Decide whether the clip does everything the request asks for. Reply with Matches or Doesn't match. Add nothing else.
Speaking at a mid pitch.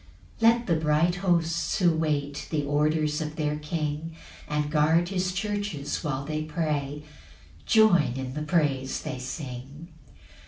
Matches